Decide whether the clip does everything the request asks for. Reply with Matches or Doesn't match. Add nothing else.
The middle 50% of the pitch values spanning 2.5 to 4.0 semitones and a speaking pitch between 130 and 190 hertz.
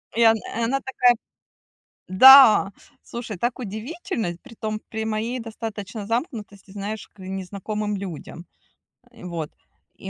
Doesn't match